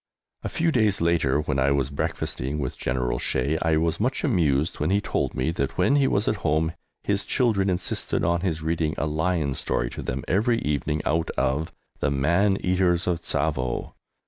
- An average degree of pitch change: Yes, average, 4.9 semitones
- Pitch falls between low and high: No, very low, 80 Hz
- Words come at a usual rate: Yes, average, 190 wpm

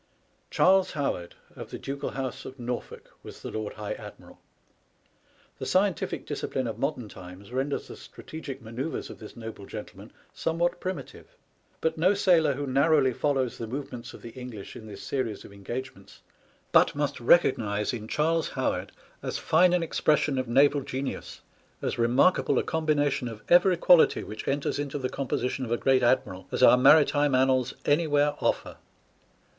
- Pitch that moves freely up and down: No, average, 4.2 semitones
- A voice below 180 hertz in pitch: Yes, low, 135 Hz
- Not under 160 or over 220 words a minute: Yes, average, 165 wpm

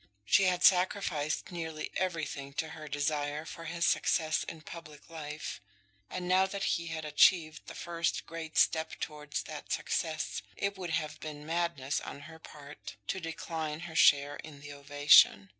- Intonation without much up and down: Yes, narrow, 2.3 semitones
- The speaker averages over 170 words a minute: No, average, 160 wpm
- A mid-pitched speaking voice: Yes, medium, 155 Hz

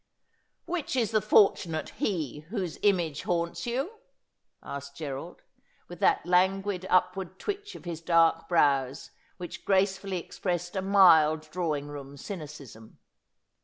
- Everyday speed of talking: No, slow, 130 wpm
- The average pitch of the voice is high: No, medium, 175 Hz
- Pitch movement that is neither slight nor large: Yes, average, 4.2 semitones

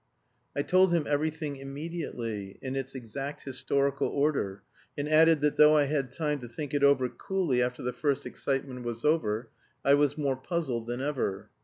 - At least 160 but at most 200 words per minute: Yes, average, 175 wpm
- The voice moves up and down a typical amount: Yes, average, 3.1 semitones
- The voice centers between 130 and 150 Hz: Yes, medium, 140 Hz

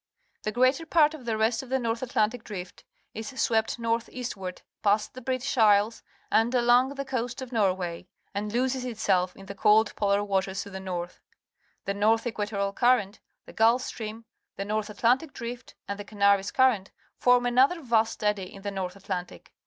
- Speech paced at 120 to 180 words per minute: No, average, 190 wpm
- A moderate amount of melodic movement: Yes, average, 3.7 semitones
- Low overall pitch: No, high, 220 Hz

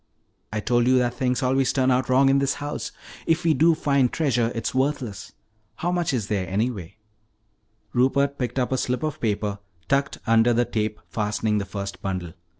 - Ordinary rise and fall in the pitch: Yes, average, 4.3 semitones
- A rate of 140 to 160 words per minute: No, average, 185 wpm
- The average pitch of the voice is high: No, low, 125 Hz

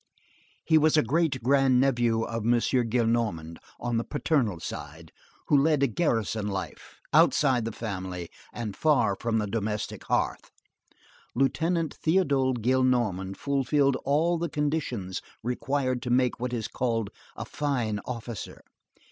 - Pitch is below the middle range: Yes, low, 125 Hz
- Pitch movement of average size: Yes, average, 4.2 semitones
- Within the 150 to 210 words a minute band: No, slow, 135 wpm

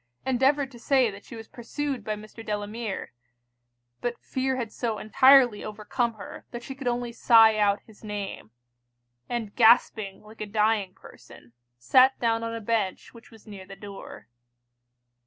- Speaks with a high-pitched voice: Yes, high, 225 Hz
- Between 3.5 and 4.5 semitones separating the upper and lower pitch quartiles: No, average, 2.7 semitones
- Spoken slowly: No, average, 160 wpm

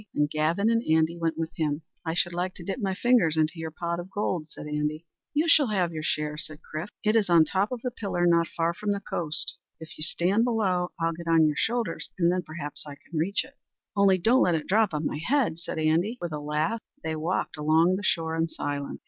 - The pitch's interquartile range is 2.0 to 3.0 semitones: No, average, 4.0 semitones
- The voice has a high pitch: No, medium, 170 Hz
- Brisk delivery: Yes, fast, 240 wpm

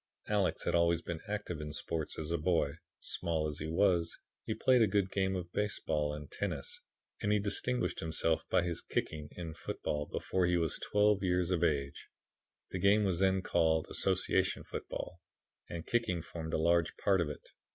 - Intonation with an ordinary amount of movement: Yes, average, 3.2 semitones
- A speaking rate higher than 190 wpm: No, average, 185 wpm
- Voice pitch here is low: Yes, very low, 85 Hz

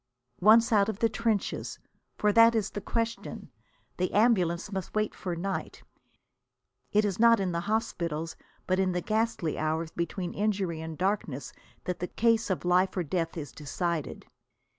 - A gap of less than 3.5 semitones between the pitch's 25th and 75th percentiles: No, average, 3.9 semitones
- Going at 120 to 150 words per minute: No, average, 160 wpm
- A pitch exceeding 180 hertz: Yes, high, 190 Hz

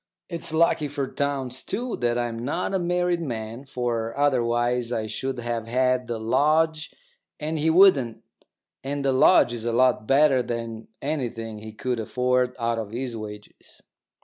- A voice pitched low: Yes, low, 125 Hz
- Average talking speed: Yes, average, 160 wpm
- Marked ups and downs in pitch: No, average, 3.6 semitones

